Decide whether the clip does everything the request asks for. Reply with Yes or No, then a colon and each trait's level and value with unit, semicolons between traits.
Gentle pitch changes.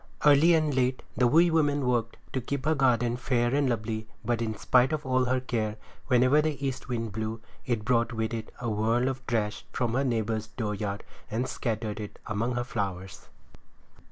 No: average, 3.1 semitones